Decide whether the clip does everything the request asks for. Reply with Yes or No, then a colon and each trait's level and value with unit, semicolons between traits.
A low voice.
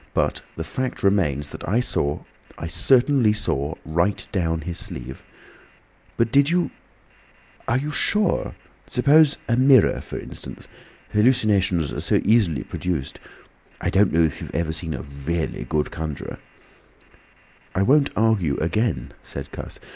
Yes: very low, 95 Hz